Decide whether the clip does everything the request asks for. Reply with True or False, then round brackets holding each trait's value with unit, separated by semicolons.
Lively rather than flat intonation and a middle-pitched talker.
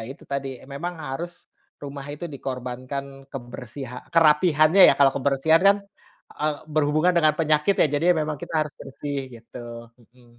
False (2.5 semitones; 145 Hz)